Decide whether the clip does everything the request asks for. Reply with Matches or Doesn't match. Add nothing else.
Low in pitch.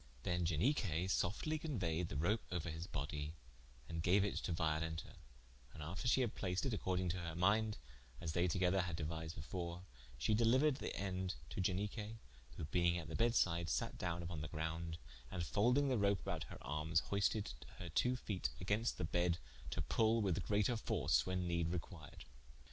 Matches